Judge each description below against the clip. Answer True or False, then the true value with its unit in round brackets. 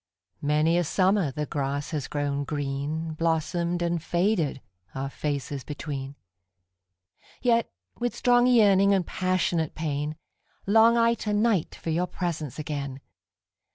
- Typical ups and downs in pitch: True (4.6 semitones)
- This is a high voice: False (155 Hz)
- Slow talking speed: True (115 wpm)